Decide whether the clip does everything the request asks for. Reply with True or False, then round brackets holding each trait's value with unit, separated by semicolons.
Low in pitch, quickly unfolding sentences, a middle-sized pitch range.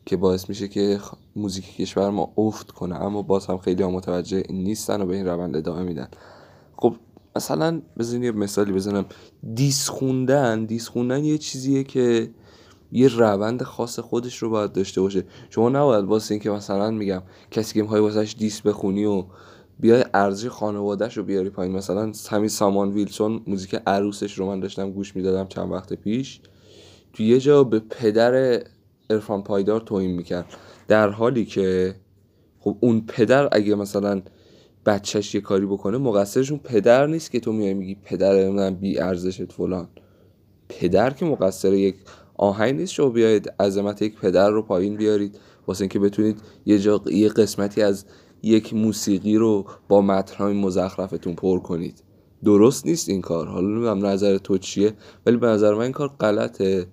False (100 Hz; 165 wpm; 2.3 semitones)